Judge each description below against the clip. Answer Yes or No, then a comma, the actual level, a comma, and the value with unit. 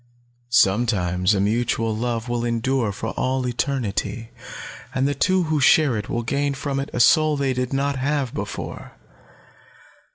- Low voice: Yes, low, 125 Hz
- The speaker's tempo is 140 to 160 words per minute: Yes, average, 155 wpm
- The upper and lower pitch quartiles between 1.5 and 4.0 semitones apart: Yes, average, 3.6 semitones